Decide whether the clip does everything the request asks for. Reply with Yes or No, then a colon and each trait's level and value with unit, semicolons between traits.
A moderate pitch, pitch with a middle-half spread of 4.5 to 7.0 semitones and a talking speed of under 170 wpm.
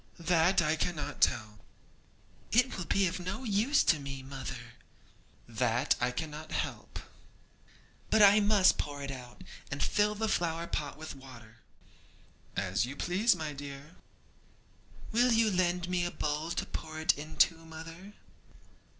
Yes: medium, 160 Hz; average, 5.2 semitones; average, 145 wpm